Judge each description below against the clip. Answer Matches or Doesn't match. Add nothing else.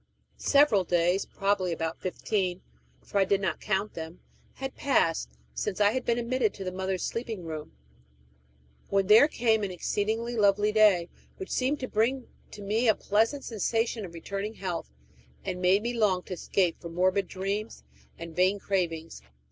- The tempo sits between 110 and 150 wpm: Doesn't match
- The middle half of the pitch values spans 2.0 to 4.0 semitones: Matches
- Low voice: Doesn't match